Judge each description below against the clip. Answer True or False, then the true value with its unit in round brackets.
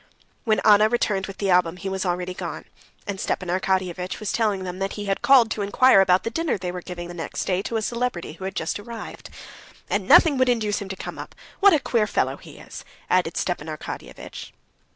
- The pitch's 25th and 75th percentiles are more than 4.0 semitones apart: False (3.5 semitones)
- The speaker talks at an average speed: False (215 wpm)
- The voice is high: True (195 Hz)